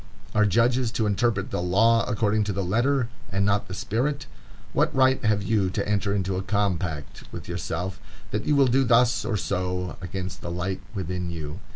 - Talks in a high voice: No, low, 100 Hz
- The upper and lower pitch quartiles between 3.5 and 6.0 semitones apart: Yes, average, 4.0 semitones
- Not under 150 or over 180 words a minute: No, average, 190 wpm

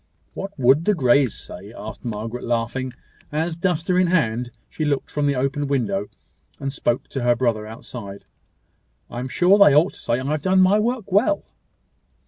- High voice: No, medium, 140 Hz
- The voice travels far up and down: Yes, wide, 6.6 semitones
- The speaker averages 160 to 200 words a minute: Yes, average, 180 wpm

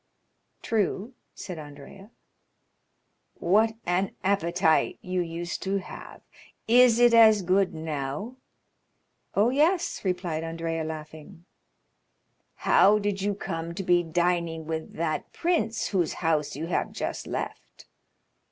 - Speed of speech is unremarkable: No, slow, 115 wpm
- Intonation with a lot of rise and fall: No, average, 4.0 semitones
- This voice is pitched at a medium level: Yes, medium, 180 Hz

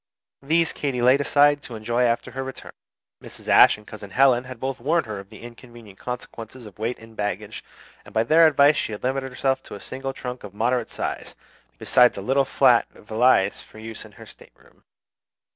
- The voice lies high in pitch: No, low, 125 Hz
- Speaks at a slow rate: No, average, 195 wpm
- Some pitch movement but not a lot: Yes, average, 3.4 semitones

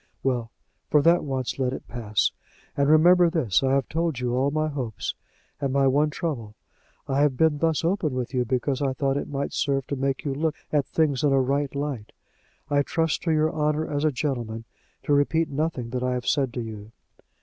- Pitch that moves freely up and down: No, average, 3.2 semitones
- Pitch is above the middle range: No, medium, 140 Hz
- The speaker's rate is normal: No, fast, 210 wpm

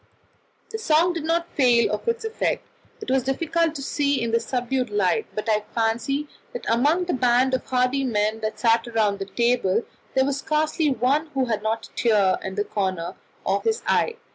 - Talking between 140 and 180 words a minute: No, average, 195 wpm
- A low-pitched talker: No, very high, 250 Hz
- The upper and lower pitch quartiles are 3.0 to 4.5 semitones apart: No, average, 5.1 semitones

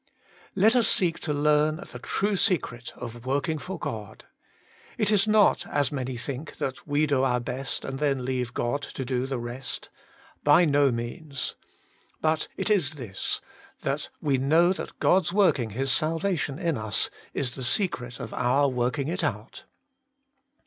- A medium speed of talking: Yes, average, 165 wpm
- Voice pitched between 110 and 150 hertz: Yes, medium, 140 Hz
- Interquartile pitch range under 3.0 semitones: No, average, 4.6 semitones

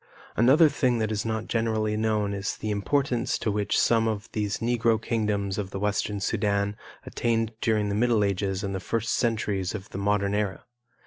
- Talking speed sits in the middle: Yes, average, 185 wpm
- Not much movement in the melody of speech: Yes, narrow, 2.1 semitones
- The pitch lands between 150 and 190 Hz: No, low, 105 Hz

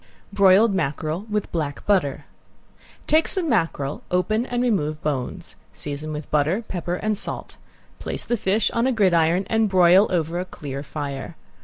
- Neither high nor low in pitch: Yes, medium, 180 Hz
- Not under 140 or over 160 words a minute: Yes, average, 155 wpm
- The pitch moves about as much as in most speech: No, wide, 5.7 semitones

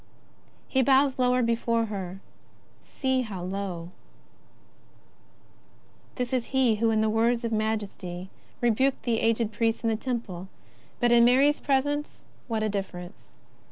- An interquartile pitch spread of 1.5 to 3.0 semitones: No, average, 3.4 semitones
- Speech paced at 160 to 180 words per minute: No, average, 140 wpm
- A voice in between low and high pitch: No, high, 230 Hz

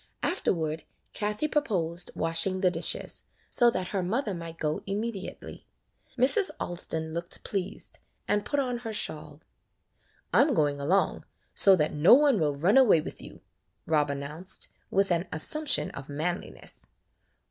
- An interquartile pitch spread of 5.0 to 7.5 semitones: Yes, wide, 5.6 semitones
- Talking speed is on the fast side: No, average, 145 wpm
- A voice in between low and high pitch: Yes, medium, 180 Hz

